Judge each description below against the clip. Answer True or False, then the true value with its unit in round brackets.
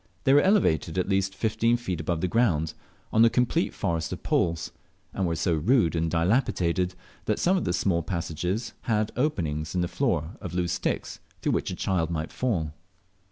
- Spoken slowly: False (190 wpm)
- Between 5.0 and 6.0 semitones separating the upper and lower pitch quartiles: True (5.3 semitones)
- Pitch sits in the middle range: False (90 Hz)